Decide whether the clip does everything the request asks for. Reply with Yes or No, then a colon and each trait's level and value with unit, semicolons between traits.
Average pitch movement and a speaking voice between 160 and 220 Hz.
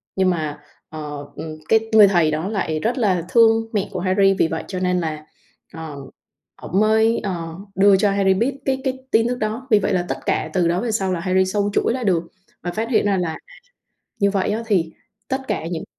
Yes: average, 4.4 semitones; high, 190 Hz